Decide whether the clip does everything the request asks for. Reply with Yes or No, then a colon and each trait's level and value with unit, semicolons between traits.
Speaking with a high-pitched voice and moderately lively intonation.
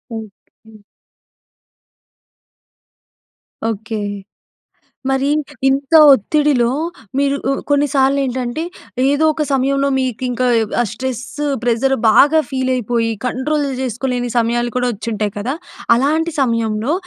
Yes: very high, 255 Hz; average, 3.2 semitones